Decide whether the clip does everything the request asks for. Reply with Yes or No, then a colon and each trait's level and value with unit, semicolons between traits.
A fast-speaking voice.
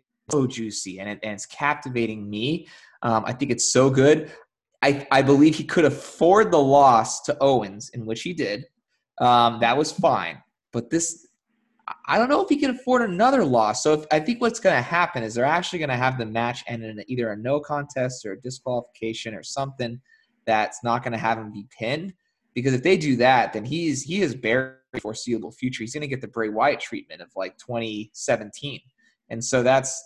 Yes: fast, 210 wpm